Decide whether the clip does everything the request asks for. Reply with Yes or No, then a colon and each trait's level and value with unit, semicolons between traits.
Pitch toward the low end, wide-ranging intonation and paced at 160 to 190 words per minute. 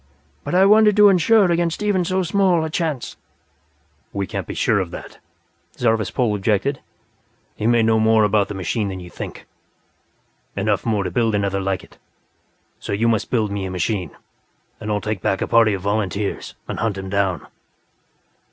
Yes: low, 110 Hz; wide, 8.1 semitones; average, 180 wpm